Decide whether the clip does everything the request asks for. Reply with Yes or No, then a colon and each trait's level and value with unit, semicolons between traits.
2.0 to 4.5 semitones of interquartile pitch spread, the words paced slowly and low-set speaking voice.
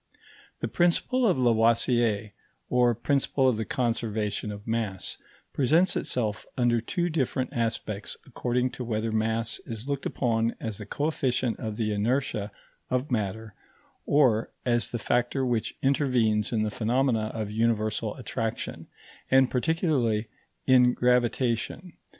Yes: average, 2.8 semitones; slow, 130 wpm; low, 120 Hz